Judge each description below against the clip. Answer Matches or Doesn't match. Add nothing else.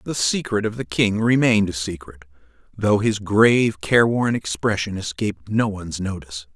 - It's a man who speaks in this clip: Matches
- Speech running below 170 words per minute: Matches